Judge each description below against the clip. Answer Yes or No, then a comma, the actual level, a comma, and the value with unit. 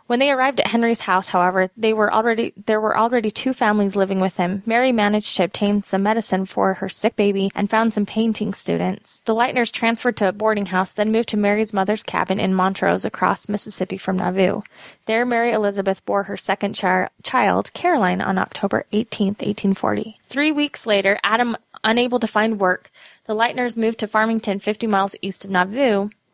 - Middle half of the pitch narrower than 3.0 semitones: Yes, narrow, 2.6 semitones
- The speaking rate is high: No, average, 190 wpm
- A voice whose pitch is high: Yes, high, 210 Hz